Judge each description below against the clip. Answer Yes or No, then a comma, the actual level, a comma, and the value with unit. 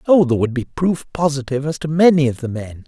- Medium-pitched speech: Yes, medium, 145 Hz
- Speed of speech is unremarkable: No, fast, 250 wpm